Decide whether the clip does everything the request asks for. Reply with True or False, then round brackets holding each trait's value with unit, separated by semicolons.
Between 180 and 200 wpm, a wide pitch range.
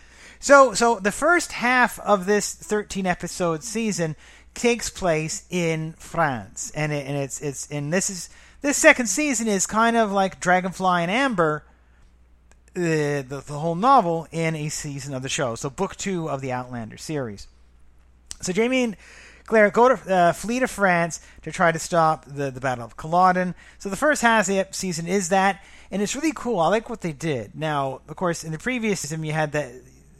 True (190 wpm; 6.1 semitones)